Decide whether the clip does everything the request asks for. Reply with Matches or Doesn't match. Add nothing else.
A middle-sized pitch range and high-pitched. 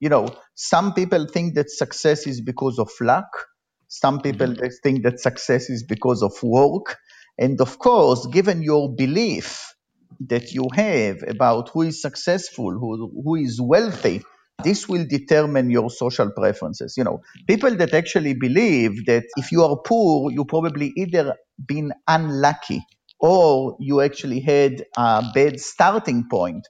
Doesn't match